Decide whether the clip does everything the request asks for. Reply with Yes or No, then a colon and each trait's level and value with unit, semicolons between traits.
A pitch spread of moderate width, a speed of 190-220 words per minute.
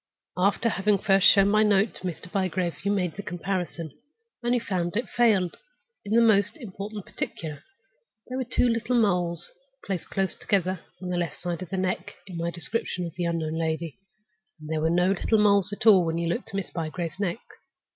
Yes: average, 3.3 semitones; average, 200 wpm